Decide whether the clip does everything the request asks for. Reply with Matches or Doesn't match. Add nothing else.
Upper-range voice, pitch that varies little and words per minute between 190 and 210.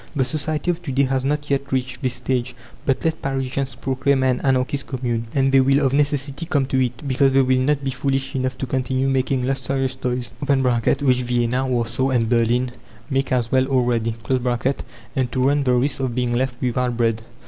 Doesn't match